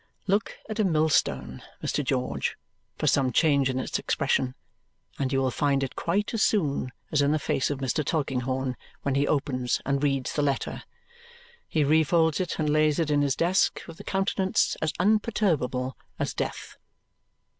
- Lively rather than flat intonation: No, average, 3.6 semitones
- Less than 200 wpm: Yes, average, 170 wpm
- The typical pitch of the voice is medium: Yes, medium, 145 Hz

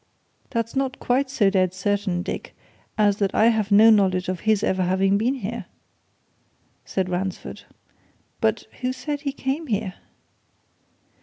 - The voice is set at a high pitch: Yes, high, 210 Hz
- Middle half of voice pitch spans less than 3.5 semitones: No, average, 4.6 semitones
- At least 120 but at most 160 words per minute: Yes, average, 145 wpm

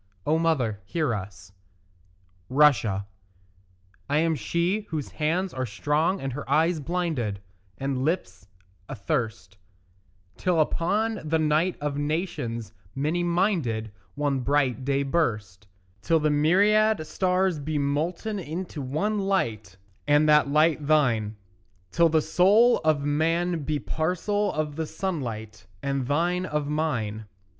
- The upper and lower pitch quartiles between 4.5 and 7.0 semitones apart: Yes, average, 4.8 semitones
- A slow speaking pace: Yes, slow, 125 wpm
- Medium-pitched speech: Yes, medium, 150 Hz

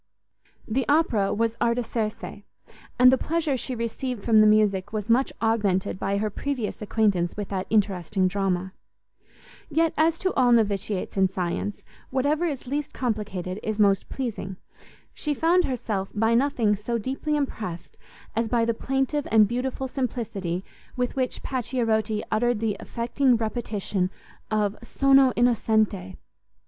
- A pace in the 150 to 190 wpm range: No, average, 140 wpm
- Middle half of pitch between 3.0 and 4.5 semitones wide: Yes, average, 4.1 semitones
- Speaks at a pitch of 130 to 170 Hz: No, high, 225 Hz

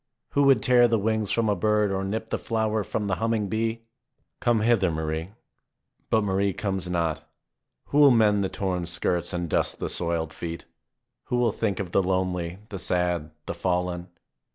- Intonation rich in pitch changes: No, average, 3.9 semitones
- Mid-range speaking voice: No, low, 100 Hz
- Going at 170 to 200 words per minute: Yes, average, 180 wpm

